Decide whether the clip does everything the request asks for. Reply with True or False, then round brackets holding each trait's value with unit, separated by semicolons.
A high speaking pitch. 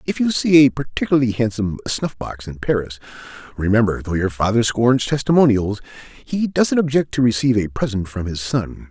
False (120 Hz)